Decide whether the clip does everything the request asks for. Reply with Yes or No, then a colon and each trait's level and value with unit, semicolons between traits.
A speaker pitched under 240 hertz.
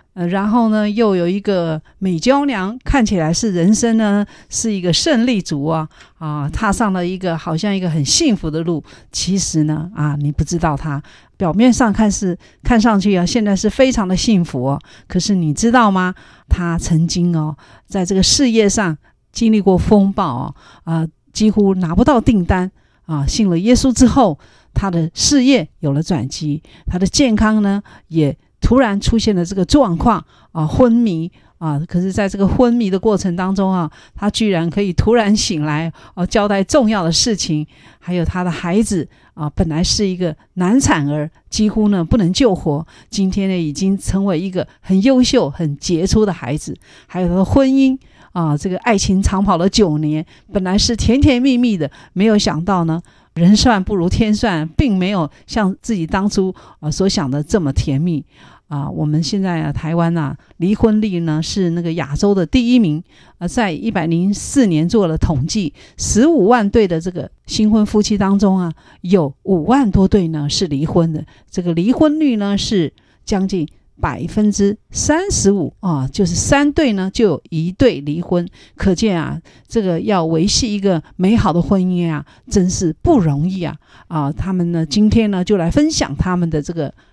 Yes: medium, 185 Hz